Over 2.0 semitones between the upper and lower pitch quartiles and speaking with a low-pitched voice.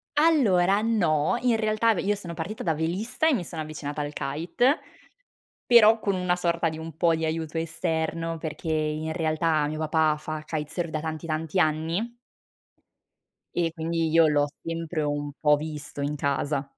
No: narrow, 2.6 semitones; medium, 160 Hz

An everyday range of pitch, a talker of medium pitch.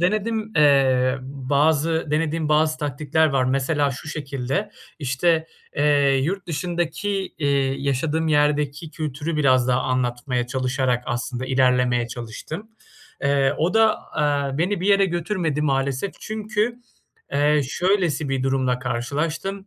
Yes: average, 3.7 semitones; medium, 145 Hz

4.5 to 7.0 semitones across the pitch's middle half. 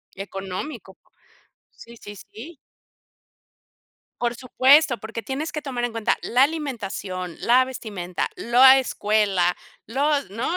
Yes: average, 4.8 semitones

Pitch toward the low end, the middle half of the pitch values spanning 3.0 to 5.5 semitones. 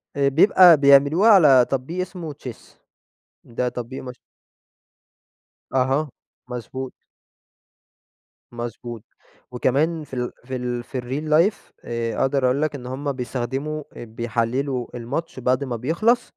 Yes: low, 130 Hz; average, 3.3 semitones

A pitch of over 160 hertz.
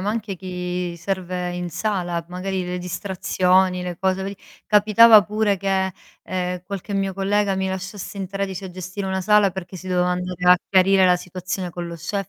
Yes: medium, 185 Hz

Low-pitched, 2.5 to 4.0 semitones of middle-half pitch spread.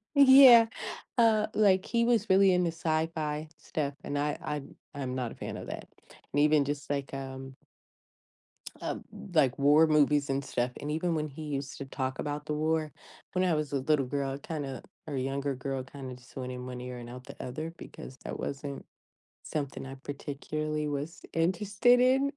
No: medium, 145 Hz; average, 3.2 semitones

